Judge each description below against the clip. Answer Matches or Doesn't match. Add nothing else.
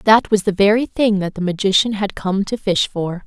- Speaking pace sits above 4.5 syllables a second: Matches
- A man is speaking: Doesn't match